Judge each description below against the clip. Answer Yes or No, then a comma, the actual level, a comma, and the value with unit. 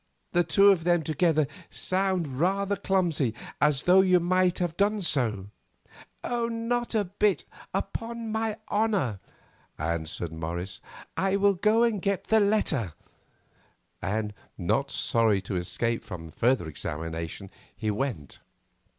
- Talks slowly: Yes, slow, 125 wpm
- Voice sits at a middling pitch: Yes, medium, 170 Hz